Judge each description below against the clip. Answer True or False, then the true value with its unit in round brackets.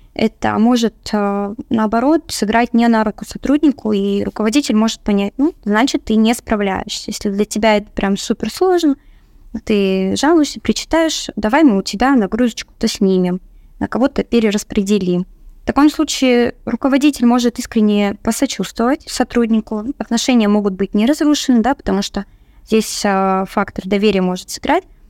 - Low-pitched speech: False (225 Hz)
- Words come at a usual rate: True (135 wpm)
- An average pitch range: True (4.0 semitones)